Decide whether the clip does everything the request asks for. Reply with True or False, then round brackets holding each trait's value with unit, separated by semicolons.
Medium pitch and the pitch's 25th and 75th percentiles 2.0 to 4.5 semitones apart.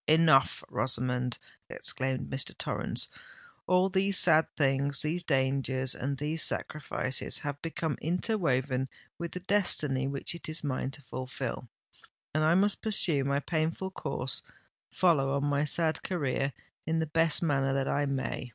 True (145 Hz; 3.6 semitones)